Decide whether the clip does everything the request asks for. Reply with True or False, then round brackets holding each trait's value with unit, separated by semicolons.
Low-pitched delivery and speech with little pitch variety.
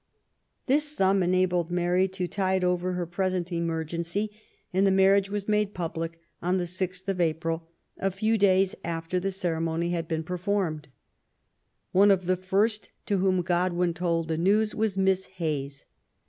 False (180 Hz; 2.3 semitones)